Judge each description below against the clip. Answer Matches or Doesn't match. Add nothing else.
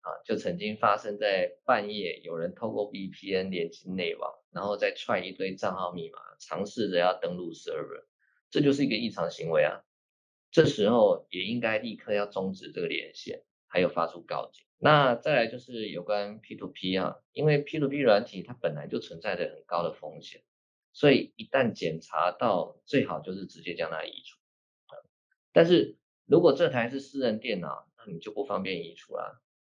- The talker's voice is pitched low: Doesn't match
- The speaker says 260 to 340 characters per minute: Matches